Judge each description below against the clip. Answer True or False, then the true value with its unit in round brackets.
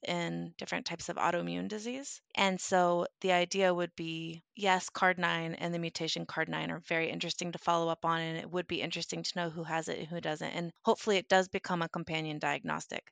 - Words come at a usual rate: False (210 wpm)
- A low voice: False (170 Hz)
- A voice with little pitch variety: True (2.0 semitones)